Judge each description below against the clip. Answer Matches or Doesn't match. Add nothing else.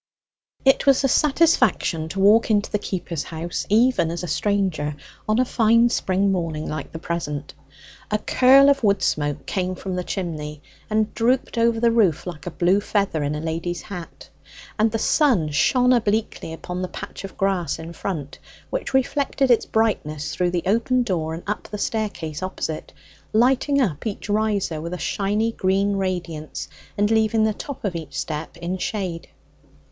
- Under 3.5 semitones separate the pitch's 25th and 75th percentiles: Doesn't match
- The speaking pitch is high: Matches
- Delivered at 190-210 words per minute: Doesn't match